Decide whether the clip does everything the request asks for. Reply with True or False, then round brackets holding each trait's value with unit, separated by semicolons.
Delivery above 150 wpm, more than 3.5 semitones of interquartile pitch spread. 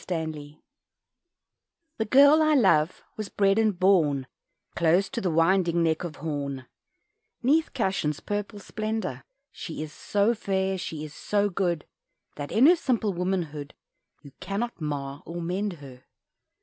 False (140 wpm; 5.1 semitones)